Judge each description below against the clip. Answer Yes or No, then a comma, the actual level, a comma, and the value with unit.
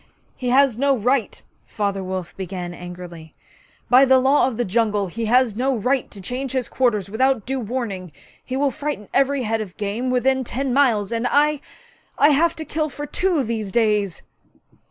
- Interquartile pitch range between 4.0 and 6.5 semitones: Yes, average, 4.6 semitones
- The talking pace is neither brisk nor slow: Yes, average, 180 wpm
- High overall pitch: Yes, high, 245 Hz